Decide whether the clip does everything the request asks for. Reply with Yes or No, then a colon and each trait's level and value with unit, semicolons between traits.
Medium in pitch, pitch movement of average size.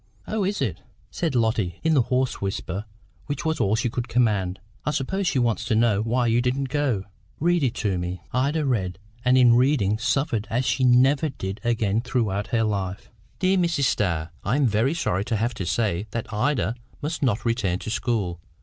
No: low, 120 Hz; average, 4.8 semitones